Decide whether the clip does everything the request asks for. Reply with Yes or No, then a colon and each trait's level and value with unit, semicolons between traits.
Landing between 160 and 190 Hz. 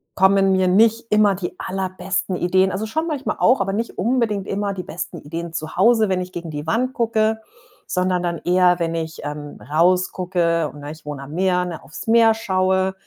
Yes: medium, 185 Hz